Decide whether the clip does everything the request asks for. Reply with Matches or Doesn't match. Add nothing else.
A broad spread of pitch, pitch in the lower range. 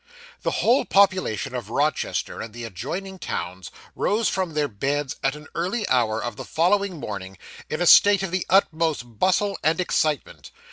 Doesn't match